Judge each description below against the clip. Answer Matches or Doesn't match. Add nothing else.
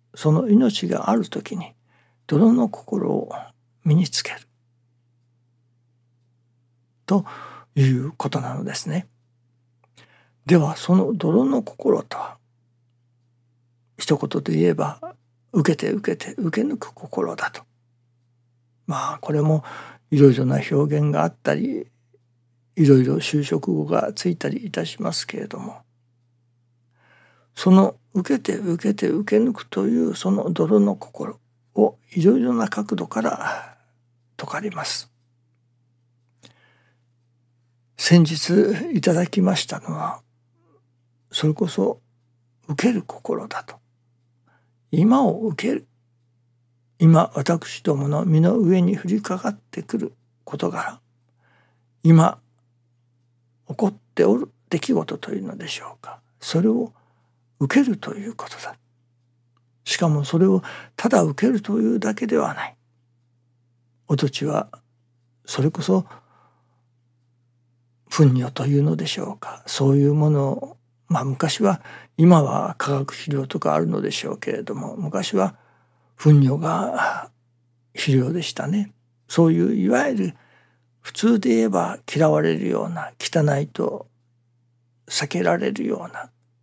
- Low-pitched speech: Matches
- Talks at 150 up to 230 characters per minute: Matches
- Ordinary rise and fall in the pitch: Doesn't match